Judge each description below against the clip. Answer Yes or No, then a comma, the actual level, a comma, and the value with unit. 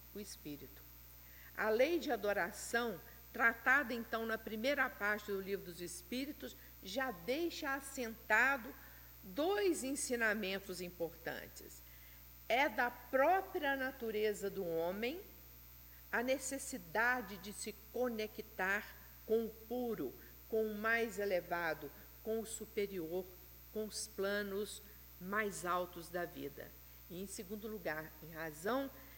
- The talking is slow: Yes, slow, 115 wpm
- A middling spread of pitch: No, wide, 5.8 semitones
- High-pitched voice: Yes, high, 215 Hz